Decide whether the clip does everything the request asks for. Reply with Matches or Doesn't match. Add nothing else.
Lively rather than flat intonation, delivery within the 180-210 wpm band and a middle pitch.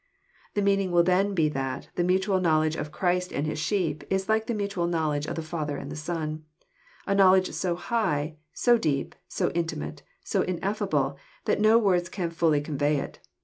Doesn't match